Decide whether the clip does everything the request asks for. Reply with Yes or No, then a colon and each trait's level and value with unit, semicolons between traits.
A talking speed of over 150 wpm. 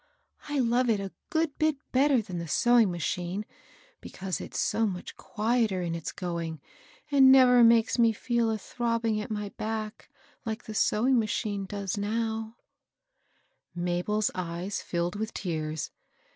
No: average, 145 wpm